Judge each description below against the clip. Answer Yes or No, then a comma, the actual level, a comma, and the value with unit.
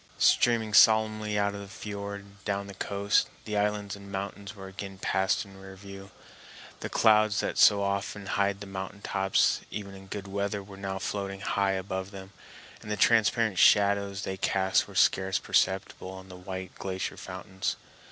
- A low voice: Yes, low, 100 Hz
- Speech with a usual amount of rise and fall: No, narrow, 1.1 semitones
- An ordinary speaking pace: Yes, average, 170 wpm